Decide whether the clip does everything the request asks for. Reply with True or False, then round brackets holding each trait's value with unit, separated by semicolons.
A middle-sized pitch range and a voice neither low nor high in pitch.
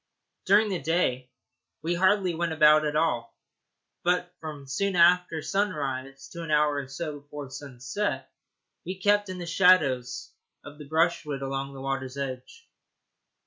True (4.7 semitones; 155 Hz)